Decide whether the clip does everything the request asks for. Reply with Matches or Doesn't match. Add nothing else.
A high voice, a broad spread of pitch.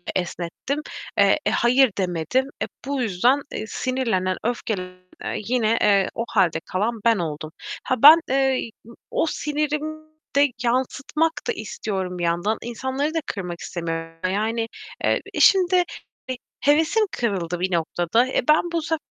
Matches